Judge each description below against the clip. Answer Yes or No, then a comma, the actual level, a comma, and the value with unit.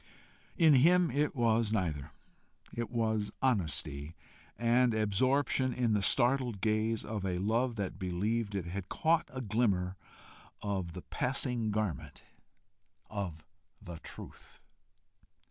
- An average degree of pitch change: Yes, average, 4.6 semitones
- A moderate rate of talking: No, slow, 120 wpm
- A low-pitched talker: Yes, low, 110 Hz